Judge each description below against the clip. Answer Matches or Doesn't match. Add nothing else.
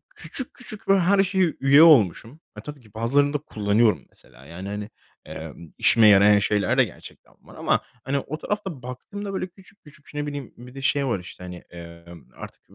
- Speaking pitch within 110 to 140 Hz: Matches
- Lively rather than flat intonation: Matches